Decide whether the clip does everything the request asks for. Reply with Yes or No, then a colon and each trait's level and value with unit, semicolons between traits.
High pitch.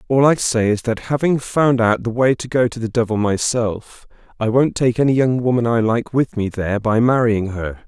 No: low, 120 Hz